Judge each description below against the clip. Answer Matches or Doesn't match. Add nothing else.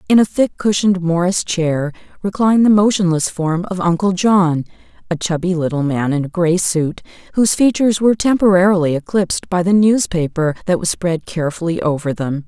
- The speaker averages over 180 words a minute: Doesn't match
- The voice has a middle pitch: Matches